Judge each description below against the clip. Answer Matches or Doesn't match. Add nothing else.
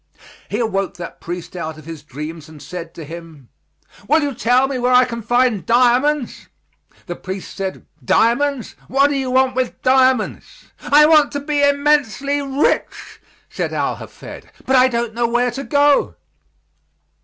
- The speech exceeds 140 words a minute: Matches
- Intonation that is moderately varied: Doesn't match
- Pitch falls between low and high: Doesn't match